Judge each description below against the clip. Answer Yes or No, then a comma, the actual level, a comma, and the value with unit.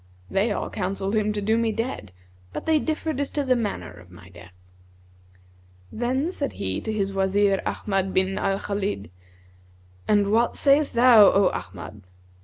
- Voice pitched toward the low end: No, high, 205 Hz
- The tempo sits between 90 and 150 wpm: No, average, 165 wpm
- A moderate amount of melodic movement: Yes, average, 3.8 semitones